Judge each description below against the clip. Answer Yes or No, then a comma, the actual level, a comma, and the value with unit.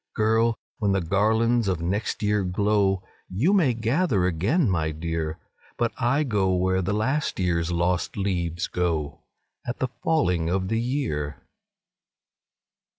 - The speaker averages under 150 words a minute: Yes, average, 140 wpm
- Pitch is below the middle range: Yes, low, 100 Hz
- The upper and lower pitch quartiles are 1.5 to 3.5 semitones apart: No, average, 4.8 semitones